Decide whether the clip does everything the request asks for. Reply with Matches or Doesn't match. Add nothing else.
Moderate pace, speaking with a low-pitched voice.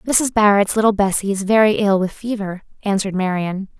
Doesn't match